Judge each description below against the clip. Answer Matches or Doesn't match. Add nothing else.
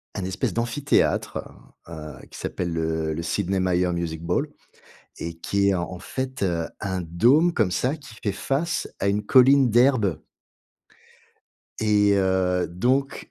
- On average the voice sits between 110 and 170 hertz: Doesn't match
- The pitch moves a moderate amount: Doesn't match